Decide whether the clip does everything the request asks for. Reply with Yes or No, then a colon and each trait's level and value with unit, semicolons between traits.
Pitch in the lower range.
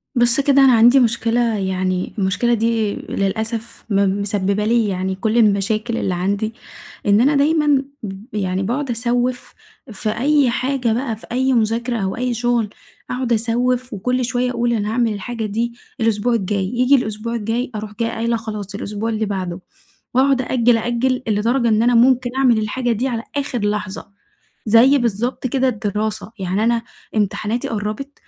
No: high, 230 Hz